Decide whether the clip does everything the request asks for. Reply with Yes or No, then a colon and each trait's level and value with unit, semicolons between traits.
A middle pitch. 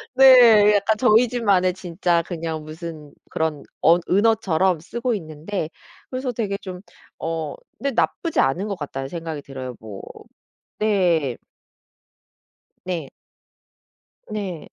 Yes: medium, 180 Hz